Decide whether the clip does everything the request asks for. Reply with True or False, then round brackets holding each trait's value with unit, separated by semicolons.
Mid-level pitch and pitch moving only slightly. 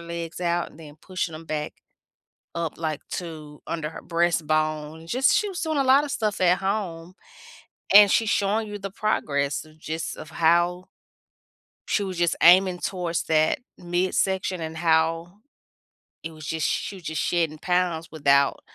False (170 Hz; 3.1 semitones)